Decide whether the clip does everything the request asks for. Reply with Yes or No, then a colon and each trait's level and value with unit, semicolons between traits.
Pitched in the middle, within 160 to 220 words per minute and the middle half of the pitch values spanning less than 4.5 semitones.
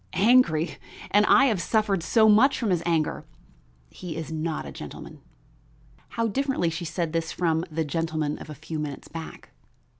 No: medium, 165 Hz; average, 175 wpm; average, 4.9 semitones